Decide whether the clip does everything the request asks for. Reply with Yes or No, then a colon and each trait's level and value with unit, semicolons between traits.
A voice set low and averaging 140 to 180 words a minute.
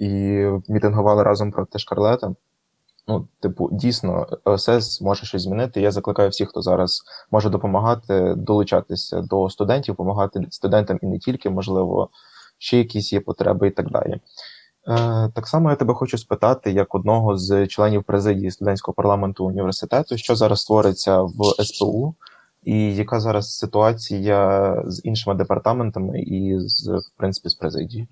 Yes: low, 100 Hz; average, 145 wpm